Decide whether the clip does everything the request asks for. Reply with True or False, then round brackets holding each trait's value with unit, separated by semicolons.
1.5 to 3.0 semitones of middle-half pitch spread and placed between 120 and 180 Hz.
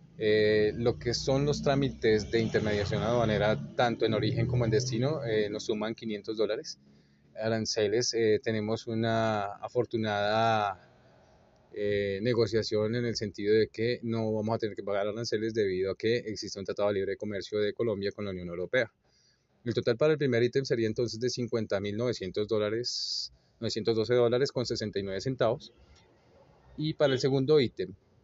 False (2.4 semitones; 110 Hz)